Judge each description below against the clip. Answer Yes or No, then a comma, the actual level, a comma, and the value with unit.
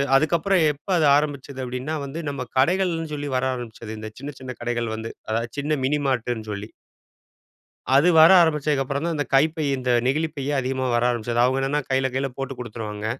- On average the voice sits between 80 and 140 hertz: Yes, low, 135 Hz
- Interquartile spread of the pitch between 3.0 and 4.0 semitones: Yes, average, 3.7 semitones